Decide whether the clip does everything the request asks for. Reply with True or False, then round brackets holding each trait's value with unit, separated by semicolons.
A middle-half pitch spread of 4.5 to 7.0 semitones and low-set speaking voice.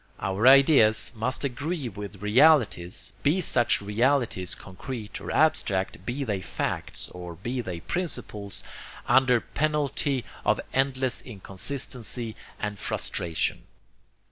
True (5.3 semitones; 120 Hz)